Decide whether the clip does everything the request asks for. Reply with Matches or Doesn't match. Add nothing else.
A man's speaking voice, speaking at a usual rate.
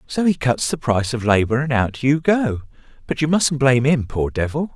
Doesn't match